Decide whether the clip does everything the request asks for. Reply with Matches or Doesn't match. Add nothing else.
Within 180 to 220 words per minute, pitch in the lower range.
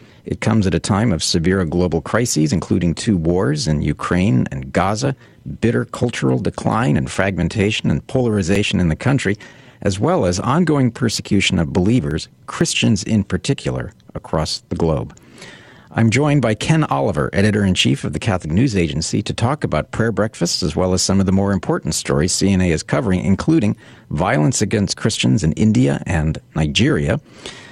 Doesn't match